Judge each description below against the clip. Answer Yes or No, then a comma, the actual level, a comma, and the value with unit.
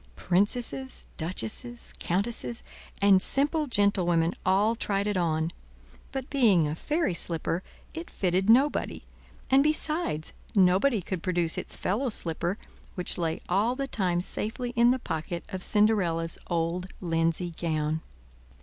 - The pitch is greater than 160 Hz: Yes, high, 190 Hz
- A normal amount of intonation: No, wide, 5.8 semitones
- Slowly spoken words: Yes, slow, 130 wpm